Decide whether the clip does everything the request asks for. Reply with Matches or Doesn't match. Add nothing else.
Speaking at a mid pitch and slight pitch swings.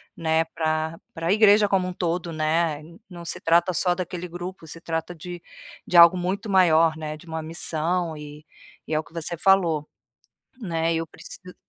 Matches